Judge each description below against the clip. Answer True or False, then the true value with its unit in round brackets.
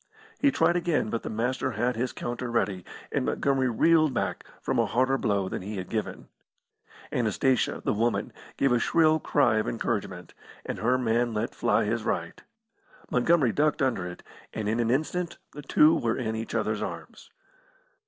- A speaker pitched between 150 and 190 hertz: False (120 Hz)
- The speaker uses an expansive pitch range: False (3.7 semitones)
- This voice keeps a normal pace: True (175 wpm)